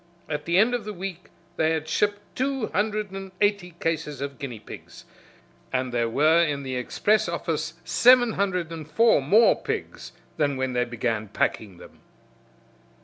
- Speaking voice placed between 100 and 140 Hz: No, medium, 160 Hz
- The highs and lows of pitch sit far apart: Yes, wide, 7.3 semitones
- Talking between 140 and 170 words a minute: Yes, average, 165 wpm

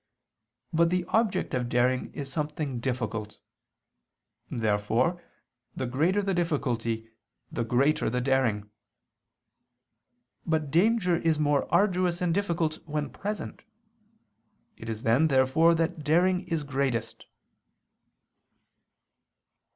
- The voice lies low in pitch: No, medium, 150 Hz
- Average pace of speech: No, slow, 105 wpm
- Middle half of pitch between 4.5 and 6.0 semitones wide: Yes, wide, 5.5 semitones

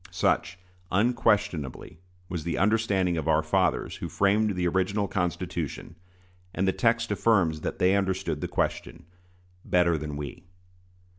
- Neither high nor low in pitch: No, very low, 90 Hz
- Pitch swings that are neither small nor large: Yes, average, 3.4 semitones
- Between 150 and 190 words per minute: No, slow, 135 wpm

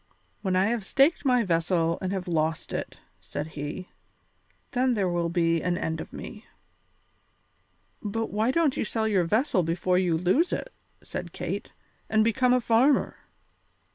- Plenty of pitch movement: Yes, wide, 5.9 semitones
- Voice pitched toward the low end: No, high, 190 Hz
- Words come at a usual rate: Yes, average, 160 wpm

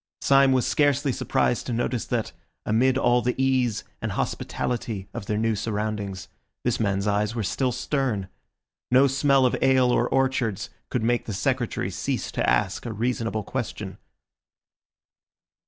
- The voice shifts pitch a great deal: No, average, 3.5 semitones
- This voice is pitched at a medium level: No, low, 120 Hz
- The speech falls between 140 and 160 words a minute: Yes, average, 150 wpm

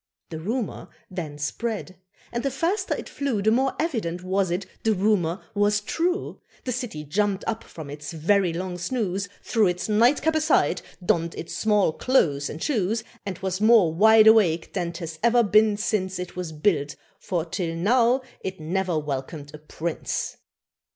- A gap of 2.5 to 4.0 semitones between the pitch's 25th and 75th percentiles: No, average, 4.9 semitones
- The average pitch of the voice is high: Yes, high, 195 Hz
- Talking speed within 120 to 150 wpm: No, average, 165 wpm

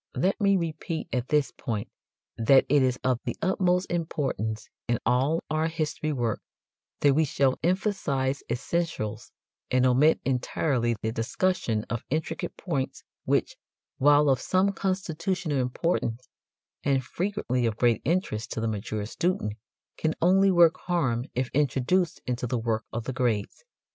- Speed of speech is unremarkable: Yes, average, 145 wpm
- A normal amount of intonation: No, wide, 5.9 semitones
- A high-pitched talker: No, low, 135 Hz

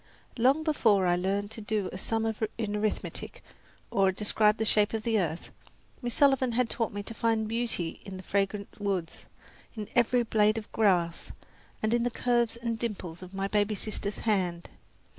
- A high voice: Yes, high, 215 Hz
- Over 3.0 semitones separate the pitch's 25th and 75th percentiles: No, average, 2.7 semitones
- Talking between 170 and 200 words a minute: Yes, average, 180 wpm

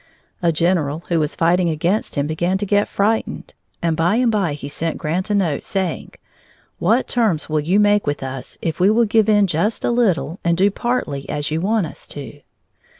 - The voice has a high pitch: No, medium, 175 Hz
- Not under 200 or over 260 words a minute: Yes, fast, 205 wpm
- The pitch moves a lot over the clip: No, average, 4.9 semitones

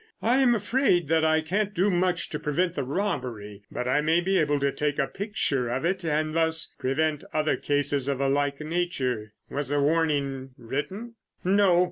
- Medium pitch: Yes, medium, 155 Hz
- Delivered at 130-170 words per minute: No, average, 185 wpm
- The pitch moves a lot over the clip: No, average, 4.3 semitones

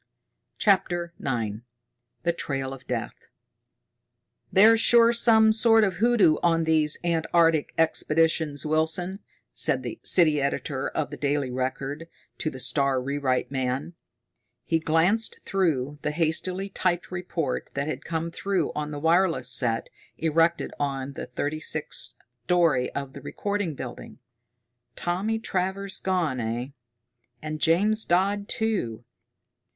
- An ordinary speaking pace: No, slow, 125 wpm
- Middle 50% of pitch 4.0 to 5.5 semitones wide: Yes, average, 4.9 semitones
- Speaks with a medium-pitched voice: Yes, medium, 160 Hz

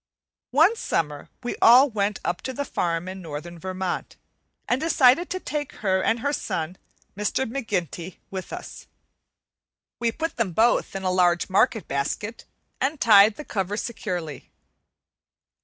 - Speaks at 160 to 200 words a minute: No, average, 145 wpm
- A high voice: Yes, high, 205 Hz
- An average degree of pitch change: No, wide, 5.8 semitones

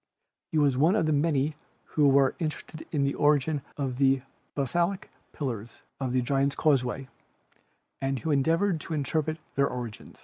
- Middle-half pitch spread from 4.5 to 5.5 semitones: No, average, 2.7 semitones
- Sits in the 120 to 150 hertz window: Yes, medium, 140 Hz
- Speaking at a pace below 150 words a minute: No, average, 160 wpm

